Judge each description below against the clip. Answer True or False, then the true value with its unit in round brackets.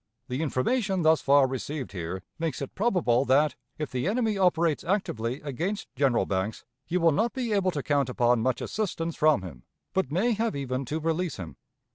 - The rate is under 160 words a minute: False (185 wpm)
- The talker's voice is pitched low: False (150 Hz)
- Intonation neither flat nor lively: False (6.4 semitones)